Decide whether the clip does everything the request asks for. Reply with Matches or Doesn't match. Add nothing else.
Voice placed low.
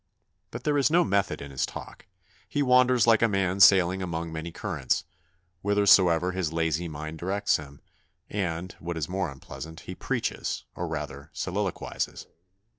Matches